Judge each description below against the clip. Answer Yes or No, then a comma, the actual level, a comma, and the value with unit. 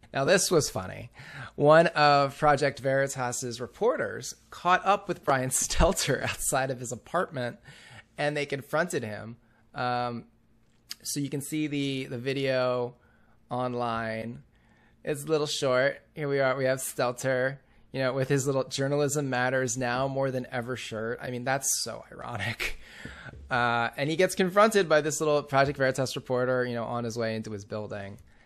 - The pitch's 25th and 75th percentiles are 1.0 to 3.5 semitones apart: Yes, average, 2.9 semitones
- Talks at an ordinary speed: Yes, average, 160 wpm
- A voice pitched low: Yes, low, 130 Hz